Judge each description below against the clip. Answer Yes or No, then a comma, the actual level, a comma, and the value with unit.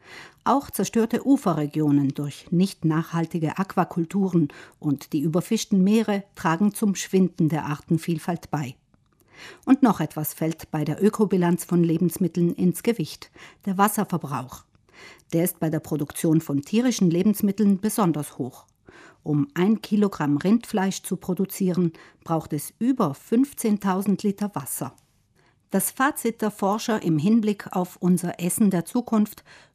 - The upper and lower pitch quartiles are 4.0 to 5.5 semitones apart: Yes, average, 4.5 semitones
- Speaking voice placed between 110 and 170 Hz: No, medium, 180 Hz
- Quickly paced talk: No, slow, 125 wpm